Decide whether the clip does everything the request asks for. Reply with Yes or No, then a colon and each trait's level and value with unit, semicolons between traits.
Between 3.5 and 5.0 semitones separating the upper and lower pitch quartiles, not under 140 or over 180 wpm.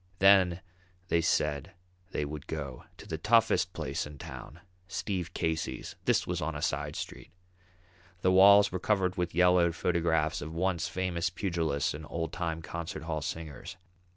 No: average, 2.7 semitones; average, 155 wpm